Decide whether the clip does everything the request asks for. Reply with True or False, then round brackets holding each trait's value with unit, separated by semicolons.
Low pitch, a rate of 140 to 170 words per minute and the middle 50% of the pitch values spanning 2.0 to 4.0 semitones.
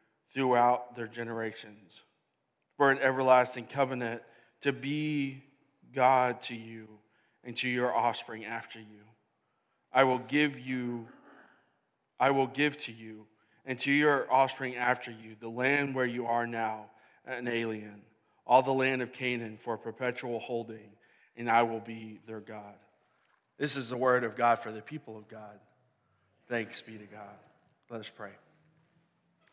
True (120 Hz; 150 wpm; 2.9 semitones)